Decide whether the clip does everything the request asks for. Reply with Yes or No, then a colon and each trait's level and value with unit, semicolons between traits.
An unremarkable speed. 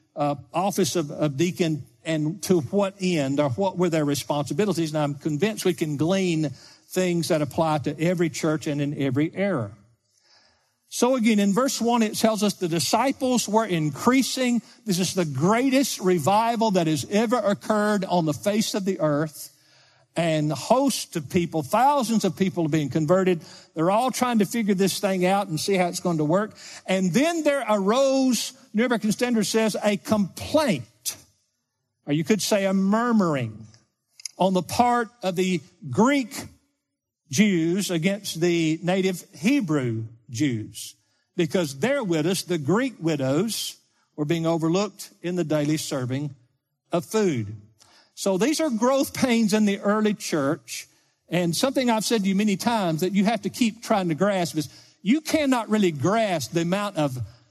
Yes: average, 170 wpm